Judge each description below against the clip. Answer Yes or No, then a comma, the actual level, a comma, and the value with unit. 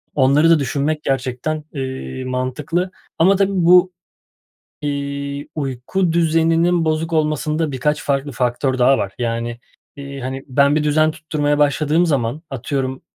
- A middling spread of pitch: Yes, average, 3.0 semitones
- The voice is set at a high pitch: No, medium, 145 Hz